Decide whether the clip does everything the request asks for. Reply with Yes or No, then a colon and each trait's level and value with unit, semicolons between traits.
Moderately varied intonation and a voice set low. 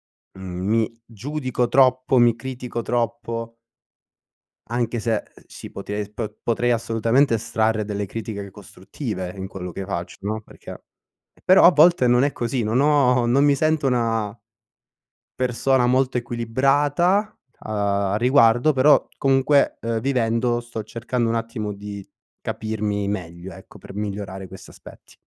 Yes: average, 3.6 semitones; low, 115 Hz